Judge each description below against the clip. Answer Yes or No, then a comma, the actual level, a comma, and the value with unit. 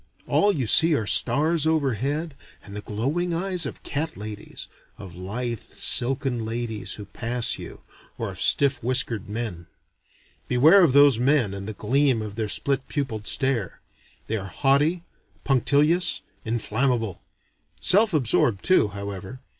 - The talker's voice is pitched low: Yes, low, 125 Hz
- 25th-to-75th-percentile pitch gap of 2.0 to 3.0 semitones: No, average, 5.2 semitones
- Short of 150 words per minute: Yes, average, 140 wpm